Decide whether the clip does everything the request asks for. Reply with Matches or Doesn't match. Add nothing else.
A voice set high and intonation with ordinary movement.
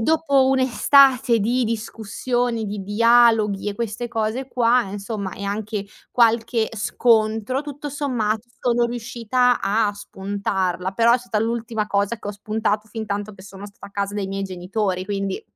Matches